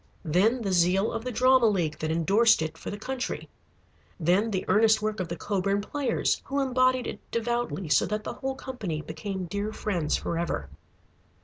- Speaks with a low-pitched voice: No, high, 205 Hz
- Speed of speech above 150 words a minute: Yes, average, 180 wpm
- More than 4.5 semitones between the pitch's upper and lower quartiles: Yes, average, 5.3 semitones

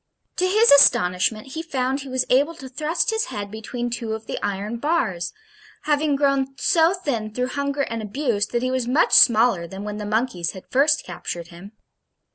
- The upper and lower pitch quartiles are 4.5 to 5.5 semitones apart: Yes, average, 5.1 semitones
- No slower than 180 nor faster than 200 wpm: Yes, average, 190 wpm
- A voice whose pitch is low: No, very high, 255 Hz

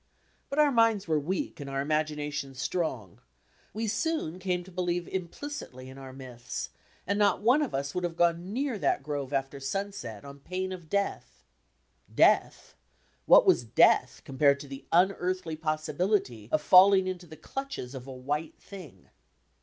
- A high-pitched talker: No, medium, 165 Hz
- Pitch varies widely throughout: Yes, wide, 5.7 semitones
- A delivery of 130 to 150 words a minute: No, average, 160 wpm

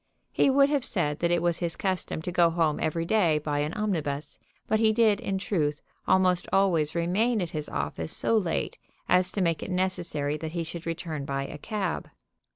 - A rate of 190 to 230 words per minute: Yes, average, 200 wpm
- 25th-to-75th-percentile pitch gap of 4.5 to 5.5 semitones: No, average, 3.8 semitones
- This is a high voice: No, medium, 170 Hz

